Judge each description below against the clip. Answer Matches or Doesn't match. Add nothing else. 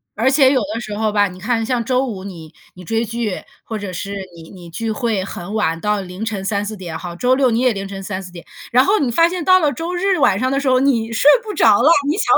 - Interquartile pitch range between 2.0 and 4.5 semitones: Doesn't match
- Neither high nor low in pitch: Doesn't match